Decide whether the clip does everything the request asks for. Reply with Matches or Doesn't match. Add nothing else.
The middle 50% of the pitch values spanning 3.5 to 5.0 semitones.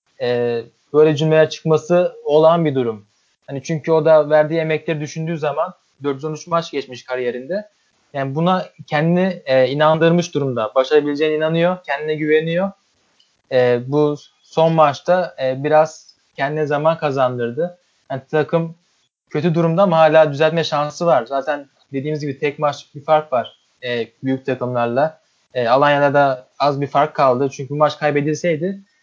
Doesn't match